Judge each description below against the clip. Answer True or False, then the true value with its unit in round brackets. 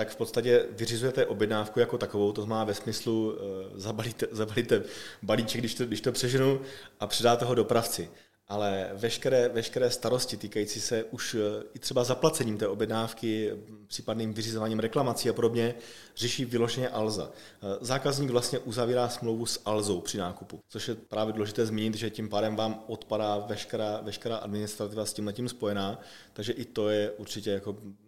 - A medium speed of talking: True (160 wpm)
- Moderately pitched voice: False (110 Hz)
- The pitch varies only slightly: True (2.2 semitones)